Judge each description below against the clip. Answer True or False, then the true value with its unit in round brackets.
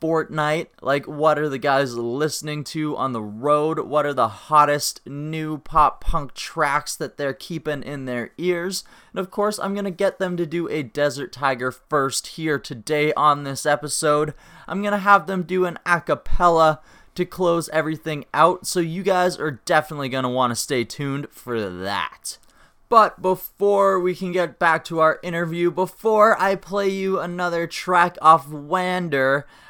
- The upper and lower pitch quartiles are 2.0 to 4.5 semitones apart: True (3.7 semitones)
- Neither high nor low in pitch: True (160 Hz)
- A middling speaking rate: True (170 wpm)